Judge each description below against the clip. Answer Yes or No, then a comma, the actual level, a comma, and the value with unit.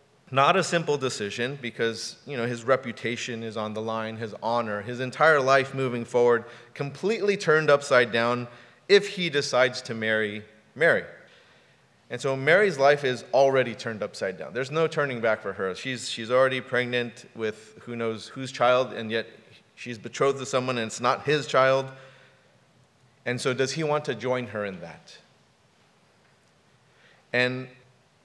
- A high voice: No, low, 125 Hz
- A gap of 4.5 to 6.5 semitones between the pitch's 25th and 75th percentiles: No, average, 2.7 semitones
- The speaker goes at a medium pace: Yes, average, 160 wpm